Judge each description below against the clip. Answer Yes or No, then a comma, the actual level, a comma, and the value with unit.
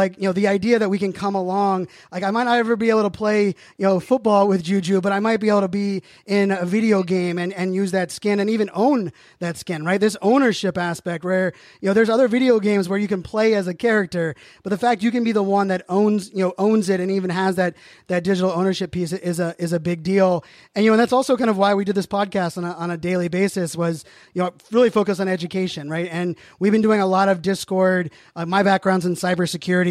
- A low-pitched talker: No, high, 195 Hz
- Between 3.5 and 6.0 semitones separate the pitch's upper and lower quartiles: No, narrow, 2.4 semitones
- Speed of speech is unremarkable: No, fast, 265 wpm